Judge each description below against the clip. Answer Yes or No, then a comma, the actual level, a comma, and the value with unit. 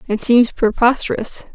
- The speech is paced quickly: No, slow, 115 wpm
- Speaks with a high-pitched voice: Yes, high, 235 Hz